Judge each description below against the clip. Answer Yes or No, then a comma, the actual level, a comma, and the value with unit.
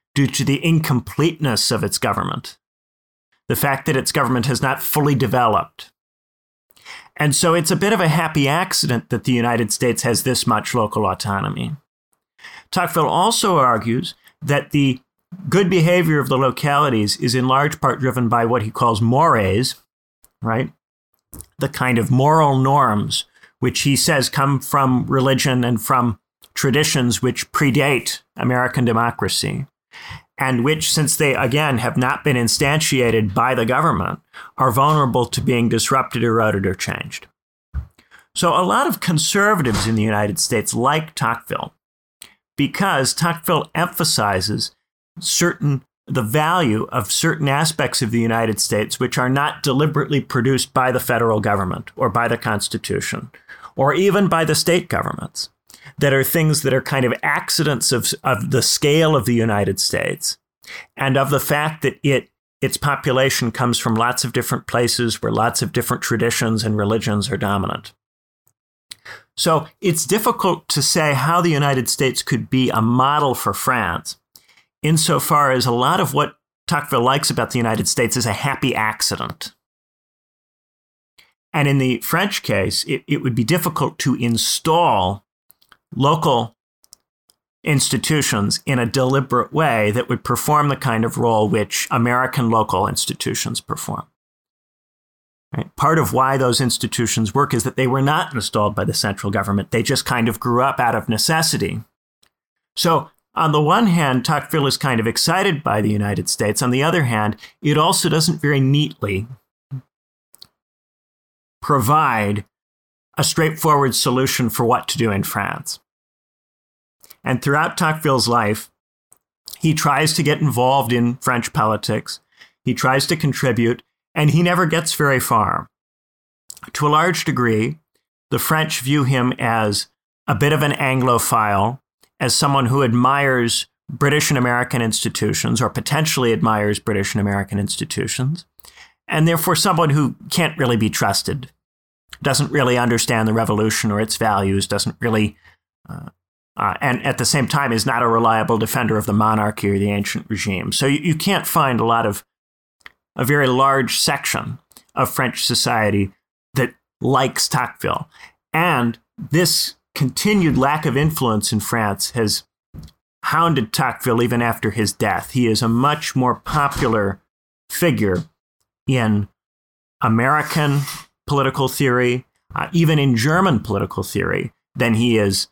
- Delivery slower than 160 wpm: Yes, average, 150 wpm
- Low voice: Yes, low, 130 Hz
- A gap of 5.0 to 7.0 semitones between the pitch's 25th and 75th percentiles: No, average, 4.5 semitones